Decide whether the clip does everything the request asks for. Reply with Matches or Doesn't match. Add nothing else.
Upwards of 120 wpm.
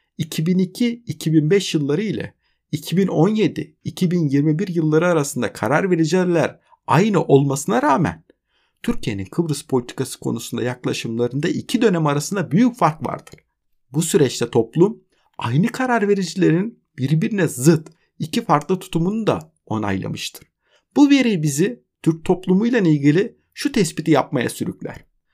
Doesn't match